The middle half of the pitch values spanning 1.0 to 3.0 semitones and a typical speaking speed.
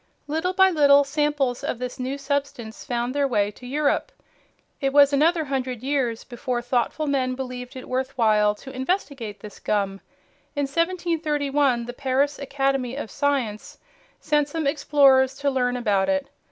Yes: narrow, 2.6 semitones; average, 155 wpm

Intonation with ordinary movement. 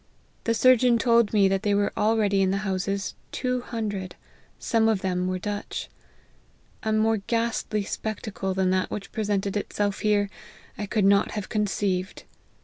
No: narrow, 2.2 semitones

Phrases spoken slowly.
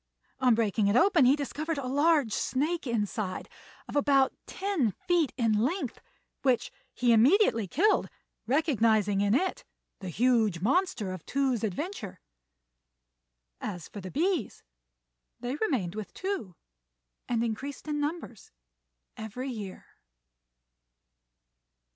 Yes: slow, 115 wpm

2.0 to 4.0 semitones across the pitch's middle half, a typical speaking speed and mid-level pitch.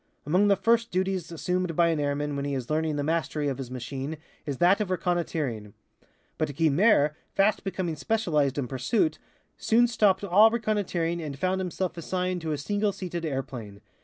No: average, 4.9 semitones; average, 175 wpm; medium, 170 Hz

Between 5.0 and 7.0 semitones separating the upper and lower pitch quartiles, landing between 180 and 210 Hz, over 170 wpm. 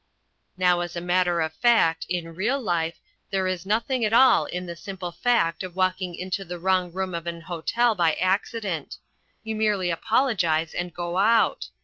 No: average, 3.3 semitones; medium, 185 Hz; average, 180 wpm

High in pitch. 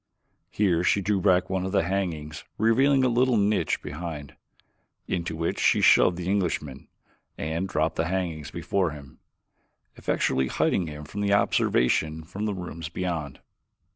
No: very low, 90 Hz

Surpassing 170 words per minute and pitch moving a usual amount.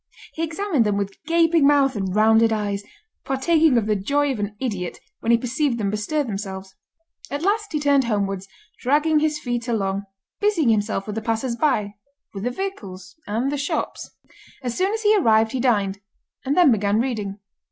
No: average, 185 wpm; wide, 6.1 semitones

